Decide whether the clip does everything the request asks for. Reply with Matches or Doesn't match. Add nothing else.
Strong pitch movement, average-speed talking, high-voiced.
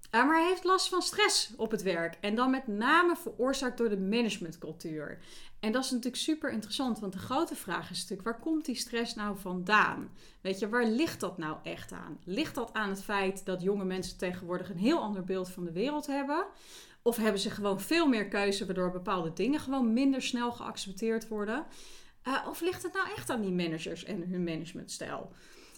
Doesn't match